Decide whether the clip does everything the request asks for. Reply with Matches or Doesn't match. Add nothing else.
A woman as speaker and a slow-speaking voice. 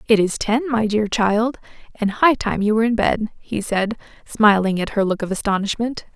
Doesn't match